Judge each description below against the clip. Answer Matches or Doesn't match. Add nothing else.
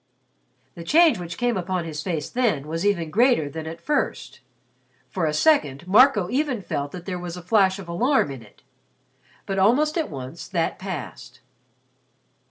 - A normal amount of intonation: Doesn't match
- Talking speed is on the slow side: Doesn't match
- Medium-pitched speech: Matches